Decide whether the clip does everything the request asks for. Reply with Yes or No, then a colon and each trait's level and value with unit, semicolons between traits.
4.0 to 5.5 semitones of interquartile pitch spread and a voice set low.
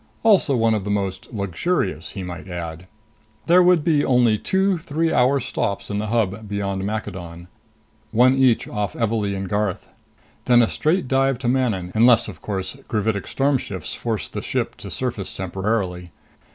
Yes: average, 5.2 semitones; low, 110 Hz